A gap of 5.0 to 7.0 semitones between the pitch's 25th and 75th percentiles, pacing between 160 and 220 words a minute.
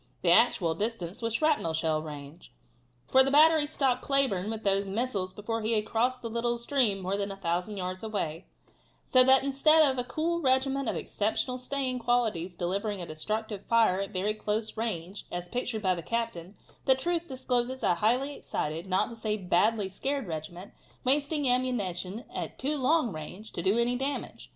Yes: wide, 5.5 semitones; average, 180 wpm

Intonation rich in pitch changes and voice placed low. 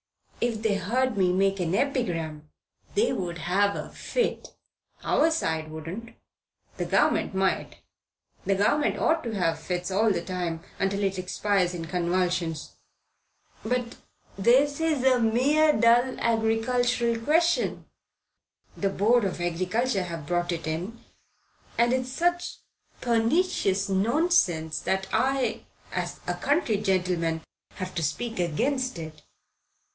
No: wide, 5.8 semitones; high, 200 Hz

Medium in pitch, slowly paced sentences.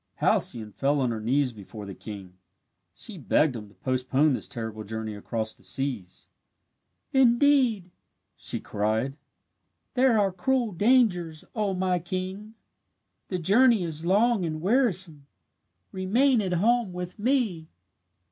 Yes: medium, 175 Hz; slow, 130 wpm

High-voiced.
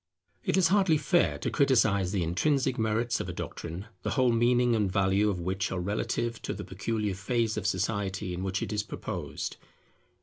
No: low, 105 Hz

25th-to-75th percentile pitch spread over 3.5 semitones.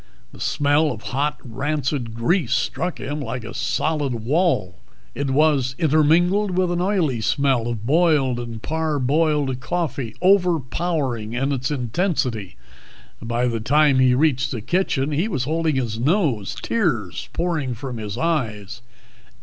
Yes: average, 5.0 semitones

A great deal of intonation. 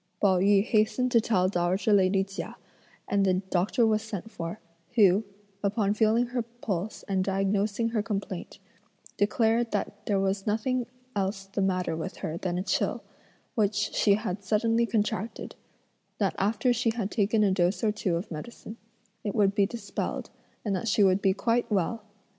No: narrow, 2.6 semitones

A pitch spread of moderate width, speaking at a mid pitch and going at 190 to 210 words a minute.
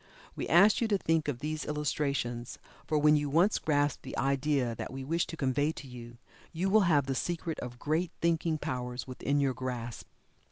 Yes: average, 3.9 semitones; medium, 145 Hz; average, 195 wpm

